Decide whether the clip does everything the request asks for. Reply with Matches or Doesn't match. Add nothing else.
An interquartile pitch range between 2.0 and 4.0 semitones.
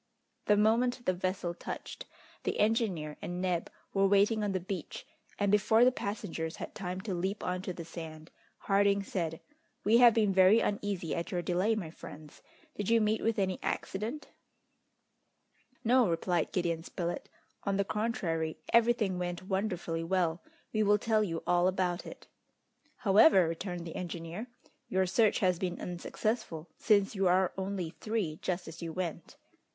Matches